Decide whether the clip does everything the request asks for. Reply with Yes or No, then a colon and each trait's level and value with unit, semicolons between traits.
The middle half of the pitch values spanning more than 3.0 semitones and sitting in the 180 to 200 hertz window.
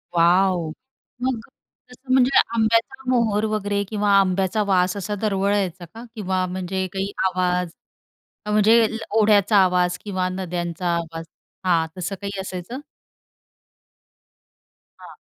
No: average, 2.7 semitones; high, 190 Hz